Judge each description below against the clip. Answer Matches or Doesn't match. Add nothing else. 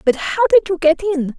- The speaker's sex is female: Matches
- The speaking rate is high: Matches